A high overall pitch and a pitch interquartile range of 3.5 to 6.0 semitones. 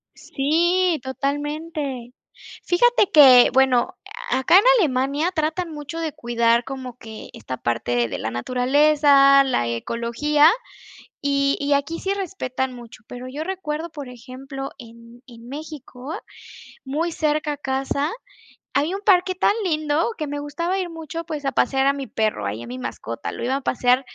Yes: very high, 280 Hz; average, 4.0 semitones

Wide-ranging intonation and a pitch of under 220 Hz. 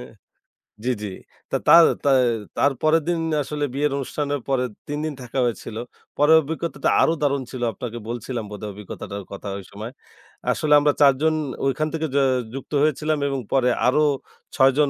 No: average, 3.7 semitones; medium, 140 Hz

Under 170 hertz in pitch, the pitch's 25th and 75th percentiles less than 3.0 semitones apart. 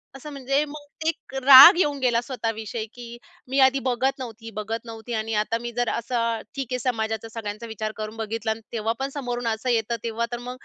No: high, 235 Hz; narrow, 2.6 semitones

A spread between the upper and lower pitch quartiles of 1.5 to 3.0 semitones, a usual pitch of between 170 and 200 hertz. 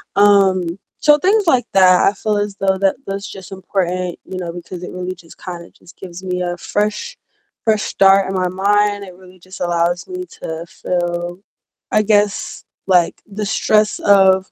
Yes: narrow, 2.4 semitones; high, 190 Hz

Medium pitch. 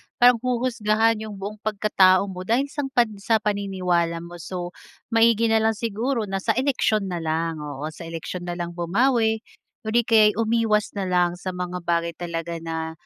No: high, 200 Hz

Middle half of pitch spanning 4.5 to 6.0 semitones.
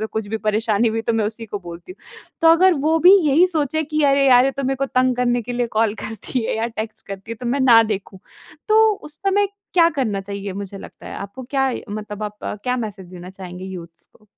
Yes: average, 4.8 semitones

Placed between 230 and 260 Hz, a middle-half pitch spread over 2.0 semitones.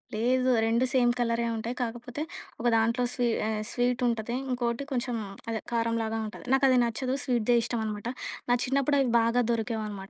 No: high, 235 Hz; narrow, 1.6 semitones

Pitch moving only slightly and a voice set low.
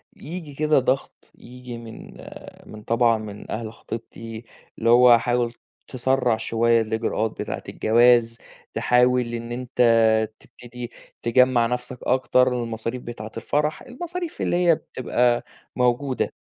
Yes: narrow, 1.7 semitones; low, 120 Hz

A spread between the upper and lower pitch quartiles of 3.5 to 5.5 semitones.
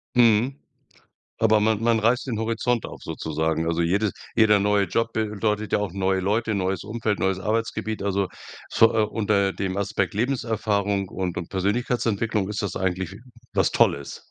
No: narrow, 2.6 semitones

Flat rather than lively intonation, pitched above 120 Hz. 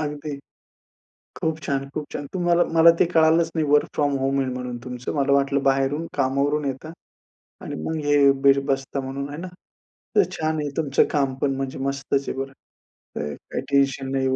Yes: narrow, 1.8 semitones; medium, 140 Hz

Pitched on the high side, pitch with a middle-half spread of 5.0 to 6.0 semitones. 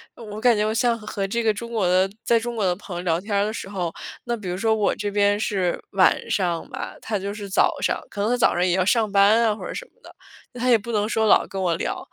No: high, 205 Hz; average, 2.8 semitones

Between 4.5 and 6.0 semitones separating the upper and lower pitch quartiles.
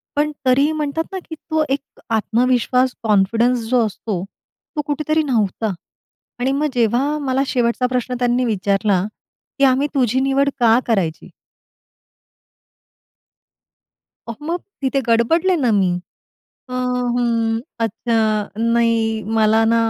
No: average, 3.6 semitones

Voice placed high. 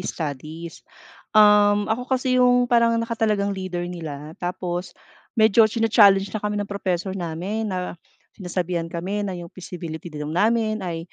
Yes: high, 195 Hz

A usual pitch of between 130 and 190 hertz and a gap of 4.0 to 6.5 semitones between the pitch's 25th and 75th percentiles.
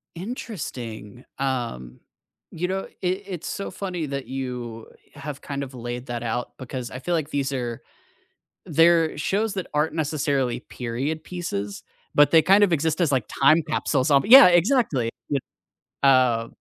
Yes: medium, 140 Hz; wide, 5.6 semitones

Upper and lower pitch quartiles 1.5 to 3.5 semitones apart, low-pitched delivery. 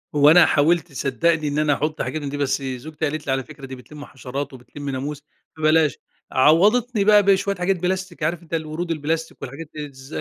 No: average, 3.2 semitones; medium, 155 Hz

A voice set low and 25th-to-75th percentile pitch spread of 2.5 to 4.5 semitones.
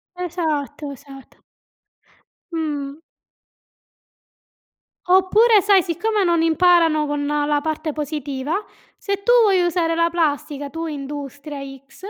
No: very high, 315 Hz; average, 3.7 semitones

